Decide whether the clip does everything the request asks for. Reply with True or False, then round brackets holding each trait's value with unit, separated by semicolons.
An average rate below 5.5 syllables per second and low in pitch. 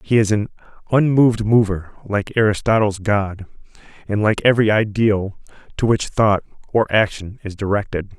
True (5.0 syllables/s; 105 Hz)